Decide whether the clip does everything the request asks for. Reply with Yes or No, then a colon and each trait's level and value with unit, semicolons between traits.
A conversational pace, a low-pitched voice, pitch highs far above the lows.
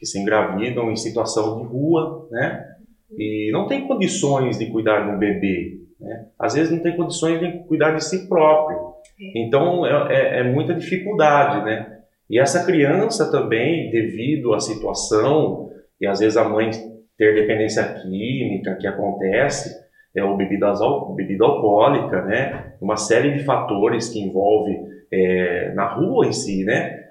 Yes: average, 155 wpm; low, 115 Hz; wide, 7.0 semitones